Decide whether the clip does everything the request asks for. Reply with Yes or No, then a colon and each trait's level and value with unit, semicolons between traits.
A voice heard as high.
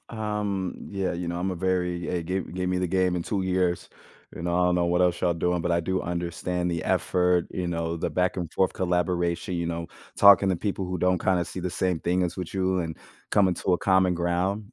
No: very low, 90 Hz